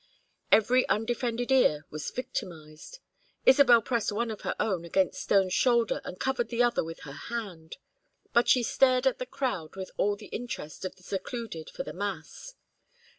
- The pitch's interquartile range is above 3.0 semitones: Yes, average, 5.2 semitones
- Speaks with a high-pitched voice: Yes, high, 225 Hz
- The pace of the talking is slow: No, average, 170 wpm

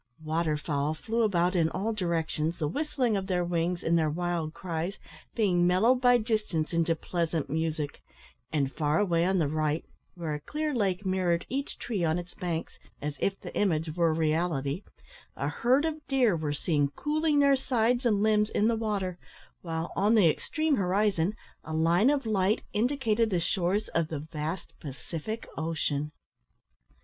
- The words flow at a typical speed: Yes, average, 170 wpm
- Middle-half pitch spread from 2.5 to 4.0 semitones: No, average, 5.2 semitones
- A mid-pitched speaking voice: Yes, medium, 175 Hz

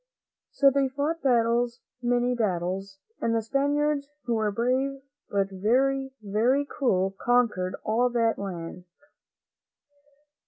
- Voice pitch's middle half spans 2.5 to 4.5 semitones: No, average, 5.1 semitones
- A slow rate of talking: Yes, slow, 115 wpm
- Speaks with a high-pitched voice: Yes, high, 240 Hz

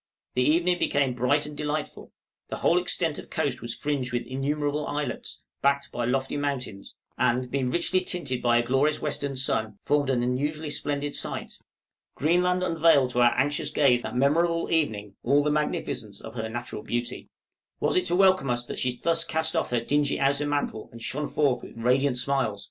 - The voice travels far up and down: No, average, 3.3 semitones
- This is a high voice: No, medium, 140 Hz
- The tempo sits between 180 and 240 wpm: Yes, average, 185 wpm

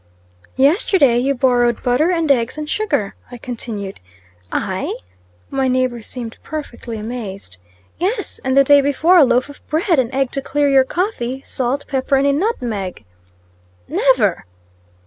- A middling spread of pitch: Yes, average, 3.2 semitones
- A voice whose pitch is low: No, very high, 265 Hz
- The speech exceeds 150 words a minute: No, average, 145 wpm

